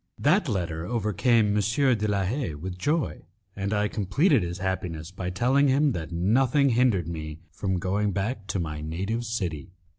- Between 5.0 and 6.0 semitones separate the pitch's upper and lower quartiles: Yes, average, 5.3 semitones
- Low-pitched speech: Yes, low, 100 Hz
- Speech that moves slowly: No, average, 170 wpm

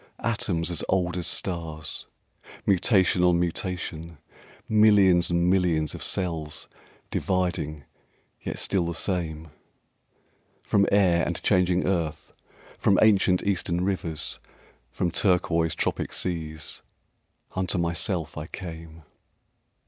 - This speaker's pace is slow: Yes, slow, 110 wpm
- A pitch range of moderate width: No, narrow, 2.3 semitones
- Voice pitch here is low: Yes, very low, 85 Hz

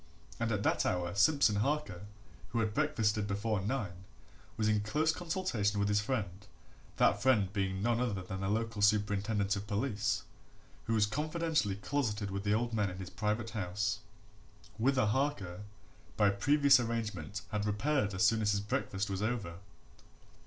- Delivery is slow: No, average, 160 wpm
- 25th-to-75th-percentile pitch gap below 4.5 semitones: Yes, average, 2.8 semitones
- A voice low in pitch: Yes, low, 105 Hz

